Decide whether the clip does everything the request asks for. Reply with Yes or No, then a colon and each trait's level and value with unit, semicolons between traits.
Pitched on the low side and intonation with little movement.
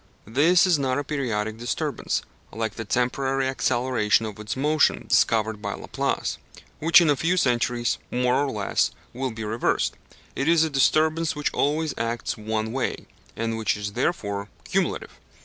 No: low, 125 Hz; average, 4.7 semitones